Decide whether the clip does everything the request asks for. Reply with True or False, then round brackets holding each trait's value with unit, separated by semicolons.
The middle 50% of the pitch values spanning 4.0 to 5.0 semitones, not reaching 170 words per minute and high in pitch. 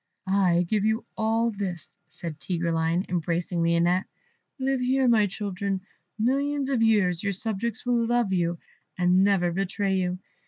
True (4.3 semitones; 145 wpm; 195 Hz)